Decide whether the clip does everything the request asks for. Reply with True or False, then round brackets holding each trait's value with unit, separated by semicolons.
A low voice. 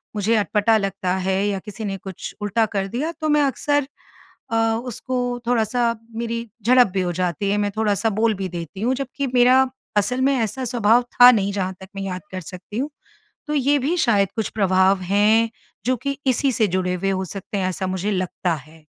False (210 Hz)